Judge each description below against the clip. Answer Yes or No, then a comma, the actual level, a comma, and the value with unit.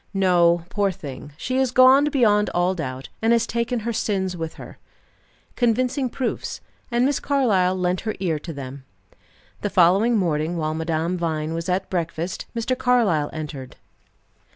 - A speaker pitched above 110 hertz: Yes, medium, 185 Hz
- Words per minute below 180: Yes, average, 155 wpm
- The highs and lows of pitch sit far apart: Yes, wide, 6.3 semitones